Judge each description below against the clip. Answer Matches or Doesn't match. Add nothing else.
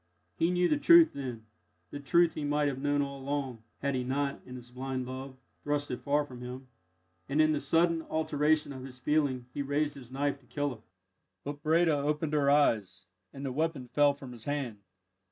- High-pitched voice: Doesn't match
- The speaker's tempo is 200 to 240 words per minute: Matches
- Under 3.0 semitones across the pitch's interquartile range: Matches